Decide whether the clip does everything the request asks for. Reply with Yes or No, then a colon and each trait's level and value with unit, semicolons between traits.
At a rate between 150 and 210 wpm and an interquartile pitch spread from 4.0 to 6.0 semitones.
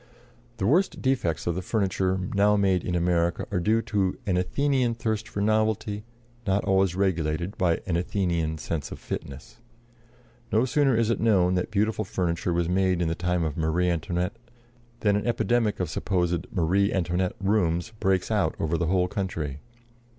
No: average, 170 wpm; average, 3.4 semitones